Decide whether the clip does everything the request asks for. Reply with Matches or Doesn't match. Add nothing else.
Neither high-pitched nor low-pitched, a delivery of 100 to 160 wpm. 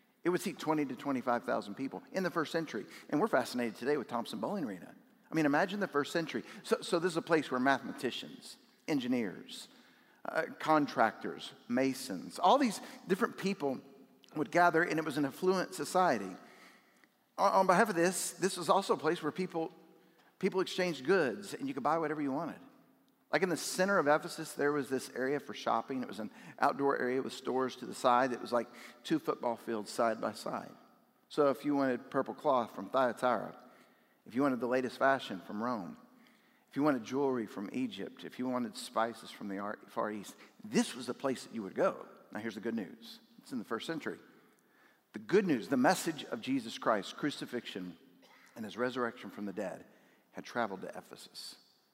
Doesn't match